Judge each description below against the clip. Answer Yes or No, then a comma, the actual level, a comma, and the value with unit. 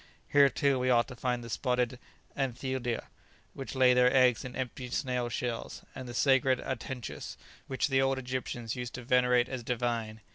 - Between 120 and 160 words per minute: No, average, 175 wpm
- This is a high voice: No, low, 125 Hz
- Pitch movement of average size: No, narrow, 1.4 semitones